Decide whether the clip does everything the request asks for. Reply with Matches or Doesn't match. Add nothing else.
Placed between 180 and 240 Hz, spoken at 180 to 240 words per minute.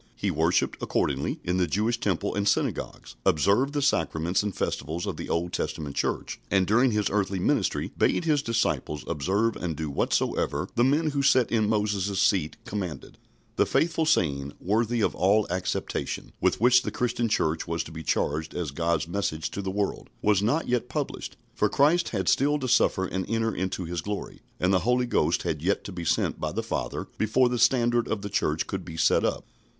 Doesn't match